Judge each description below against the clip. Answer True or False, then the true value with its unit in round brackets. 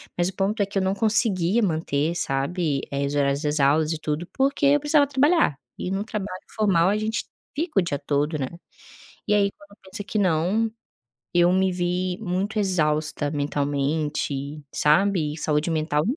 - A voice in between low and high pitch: True (175 Hz)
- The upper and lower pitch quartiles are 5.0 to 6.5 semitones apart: True (5.3 semitones)